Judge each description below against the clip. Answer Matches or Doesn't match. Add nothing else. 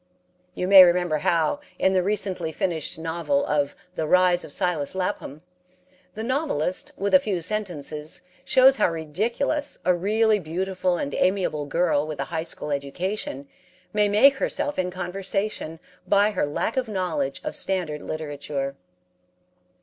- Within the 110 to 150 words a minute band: Matches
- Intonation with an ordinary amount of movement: Matches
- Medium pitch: Matches